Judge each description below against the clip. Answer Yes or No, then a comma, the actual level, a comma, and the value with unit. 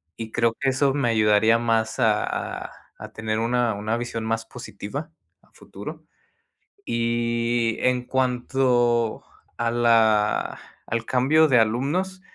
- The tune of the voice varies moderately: No, narrow, 1.9 semitones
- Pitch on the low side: Yes, low, 120 Hz